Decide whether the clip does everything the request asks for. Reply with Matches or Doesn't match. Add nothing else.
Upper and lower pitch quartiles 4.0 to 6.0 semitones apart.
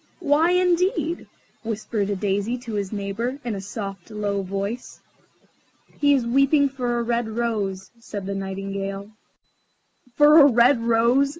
Matches